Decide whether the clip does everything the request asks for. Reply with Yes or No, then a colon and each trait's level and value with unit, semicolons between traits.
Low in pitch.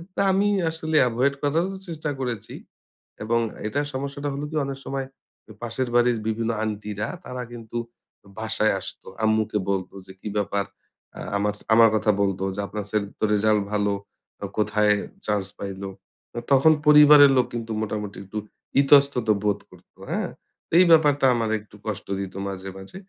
Yes: low, 110 Hz